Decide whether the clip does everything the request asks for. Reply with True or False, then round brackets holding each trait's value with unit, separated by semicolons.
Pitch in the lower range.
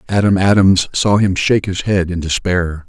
True (95 Hz)